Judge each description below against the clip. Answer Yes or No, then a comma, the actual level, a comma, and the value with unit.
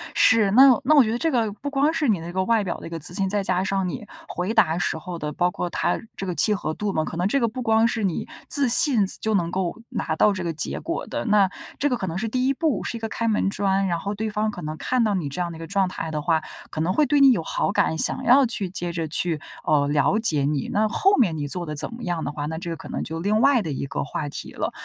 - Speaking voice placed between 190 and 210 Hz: Yes, high, 195 Hz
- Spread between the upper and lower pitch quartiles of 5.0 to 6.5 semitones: Yes, wide, 5.6 semitones